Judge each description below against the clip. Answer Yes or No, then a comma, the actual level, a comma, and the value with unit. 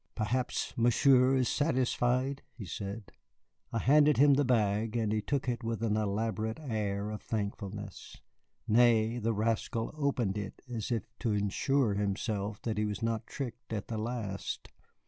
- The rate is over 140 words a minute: Yes, average, 155 wpm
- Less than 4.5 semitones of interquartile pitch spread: Yes, average, 3.0 semitones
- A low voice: Yes, low, 115 Hz